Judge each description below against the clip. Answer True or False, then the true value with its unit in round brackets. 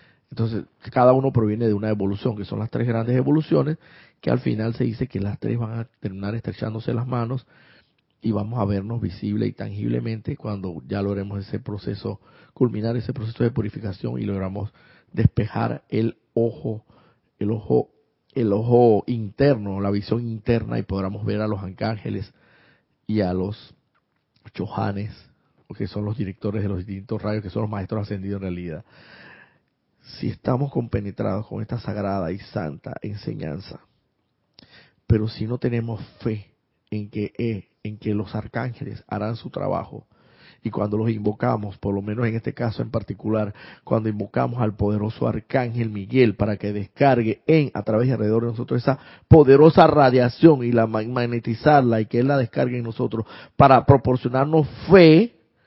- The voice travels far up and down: False (2.9 semitones)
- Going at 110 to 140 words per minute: False (160 wpm)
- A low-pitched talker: True (110 Hz)